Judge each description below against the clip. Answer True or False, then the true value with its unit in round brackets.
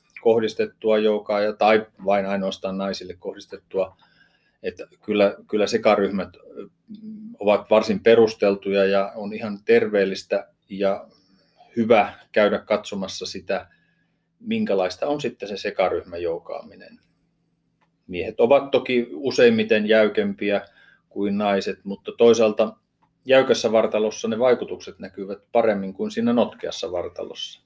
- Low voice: True (110 Hz)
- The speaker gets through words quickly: False (105 wpm)